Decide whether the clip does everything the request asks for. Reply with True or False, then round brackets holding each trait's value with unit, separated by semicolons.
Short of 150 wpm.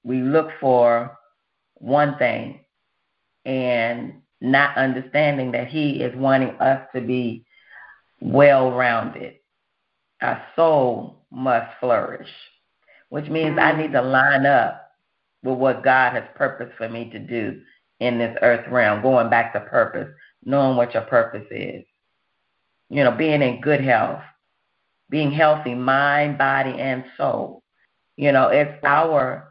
True (135 wpm)